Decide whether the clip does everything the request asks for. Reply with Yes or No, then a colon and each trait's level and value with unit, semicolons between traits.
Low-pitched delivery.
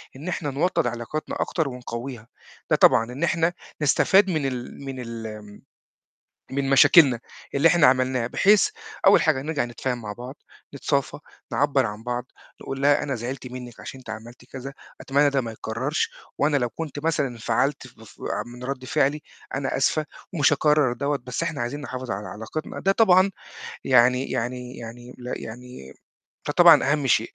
Yes: low, 130 Hz